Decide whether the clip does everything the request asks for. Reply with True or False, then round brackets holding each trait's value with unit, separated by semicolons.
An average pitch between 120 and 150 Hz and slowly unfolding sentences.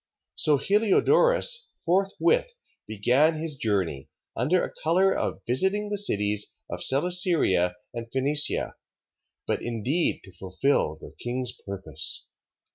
True (140 Hz; 120 wpm)